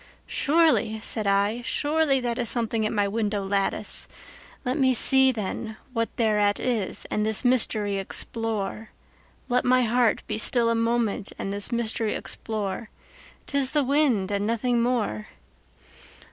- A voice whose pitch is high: Yes, high, 230 Hz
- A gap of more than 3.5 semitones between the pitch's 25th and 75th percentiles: No, average, 3.2 semitones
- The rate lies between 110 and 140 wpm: Yes, slow, 135 wpm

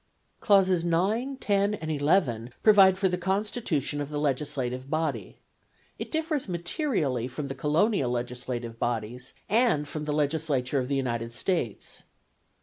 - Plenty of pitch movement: Yes, wide, 7.2 semitones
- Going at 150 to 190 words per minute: No, average, 140 wpm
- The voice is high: No, medium, 150 Hz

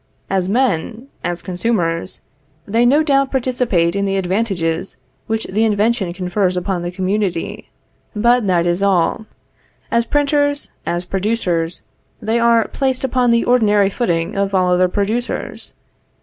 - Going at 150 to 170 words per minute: No, slow, 135 wpm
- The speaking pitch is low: No, high, 200 Hz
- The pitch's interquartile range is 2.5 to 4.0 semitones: No, average, 4.7 semitones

